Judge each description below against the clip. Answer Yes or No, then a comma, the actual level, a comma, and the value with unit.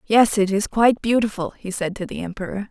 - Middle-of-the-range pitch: No, high, 205 Hz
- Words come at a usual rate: No, fast, 220 wpm